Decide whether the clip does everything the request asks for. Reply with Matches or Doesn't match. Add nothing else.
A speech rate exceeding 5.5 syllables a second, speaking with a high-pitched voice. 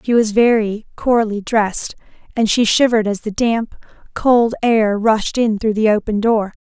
Doesn't match